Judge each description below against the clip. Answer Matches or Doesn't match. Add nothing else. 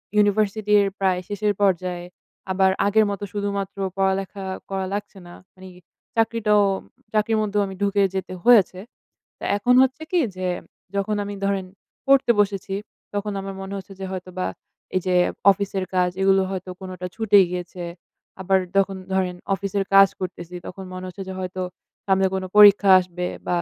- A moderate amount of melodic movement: Doesn't match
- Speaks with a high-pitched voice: Matches